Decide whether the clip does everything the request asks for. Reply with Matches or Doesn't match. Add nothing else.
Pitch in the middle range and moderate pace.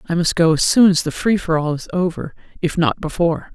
Doesn't match